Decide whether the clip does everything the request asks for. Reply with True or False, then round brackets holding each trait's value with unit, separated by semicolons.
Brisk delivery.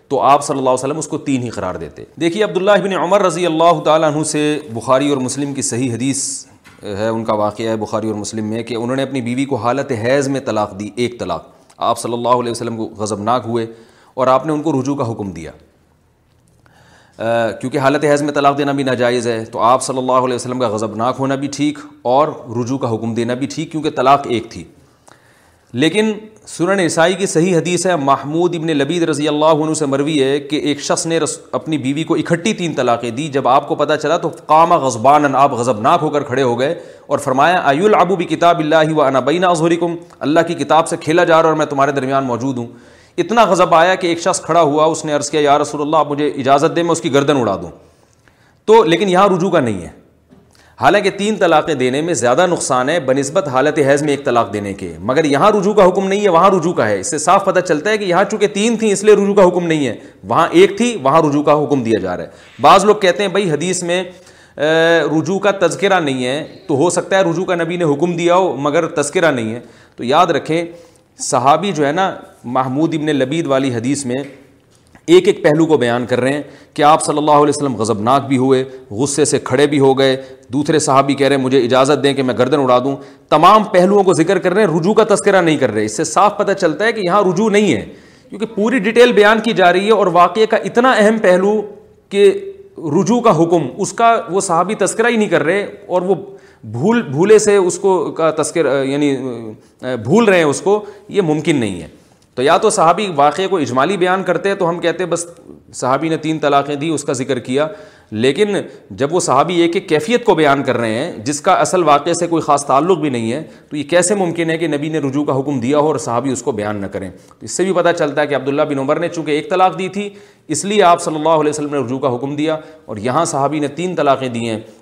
True (240 wpm)